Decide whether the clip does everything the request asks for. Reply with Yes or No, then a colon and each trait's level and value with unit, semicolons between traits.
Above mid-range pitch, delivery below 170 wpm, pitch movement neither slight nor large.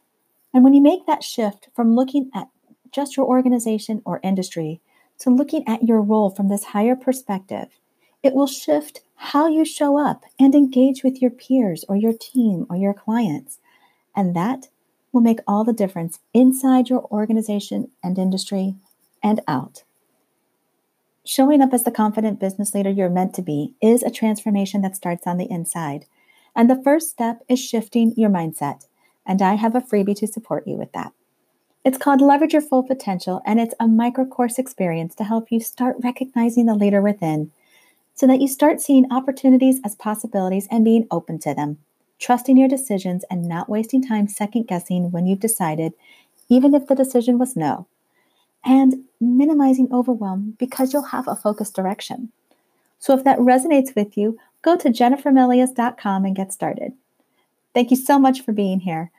No: high, 230 Hz; average, 175 wpm; average, 4.6 semitones